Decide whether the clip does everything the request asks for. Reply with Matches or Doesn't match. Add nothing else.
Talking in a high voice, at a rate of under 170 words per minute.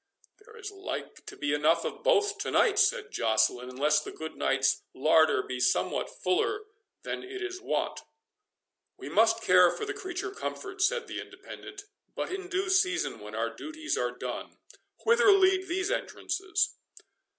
Matches